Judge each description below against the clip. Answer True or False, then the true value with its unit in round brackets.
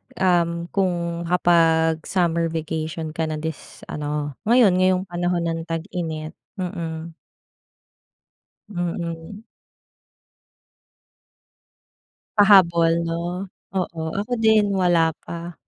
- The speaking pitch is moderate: True (170 Hz)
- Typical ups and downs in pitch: False (1.9 semitones)